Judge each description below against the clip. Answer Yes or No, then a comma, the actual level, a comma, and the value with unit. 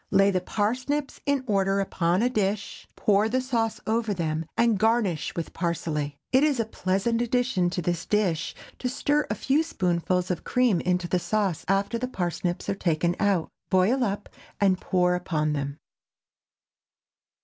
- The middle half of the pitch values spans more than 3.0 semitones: Yes, average, 4.8 semitones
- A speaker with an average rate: Yes, average, 160 wpm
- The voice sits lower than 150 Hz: No, high, 195 Hz